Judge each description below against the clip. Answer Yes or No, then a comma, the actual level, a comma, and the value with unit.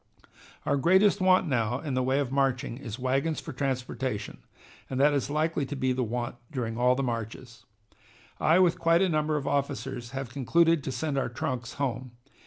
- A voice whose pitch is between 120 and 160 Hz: Yes, low, 135 Hz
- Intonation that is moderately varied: Yes, average, 3.5 semitones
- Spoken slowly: No, average, 190 wpm